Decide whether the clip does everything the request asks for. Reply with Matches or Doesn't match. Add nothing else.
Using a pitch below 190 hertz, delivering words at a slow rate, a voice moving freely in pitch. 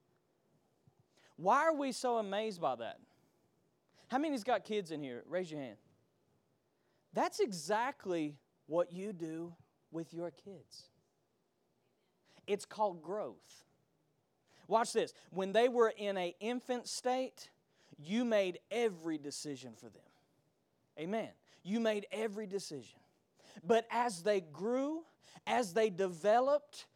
Doesn't match